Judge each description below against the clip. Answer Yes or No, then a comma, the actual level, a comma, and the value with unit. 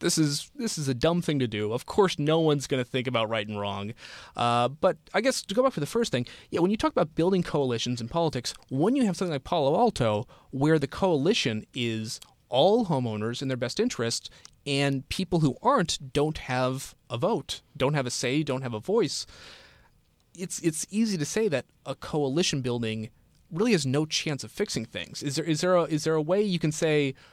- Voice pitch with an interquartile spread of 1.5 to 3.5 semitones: No, wide, 5.5 semitones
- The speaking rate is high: Yes, fast, 220 wpm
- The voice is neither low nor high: Yes, medium, 145 Hz